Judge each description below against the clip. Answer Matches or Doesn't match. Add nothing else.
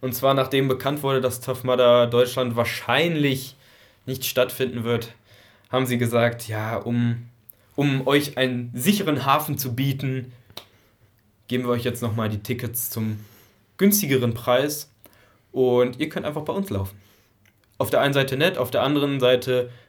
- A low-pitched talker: Matches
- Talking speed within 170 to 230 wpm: Doesn't match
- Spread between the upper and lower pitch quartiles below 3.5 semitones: Matches